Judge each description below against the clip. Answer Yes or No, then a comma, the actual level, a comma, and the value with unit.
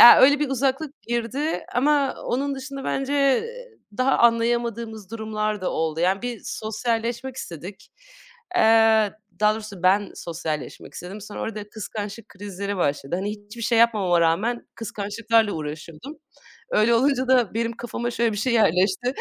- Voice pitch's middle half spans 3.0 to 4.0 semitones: Yes, average, 3.6 semitones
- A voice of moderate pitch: No, high, 225 Hz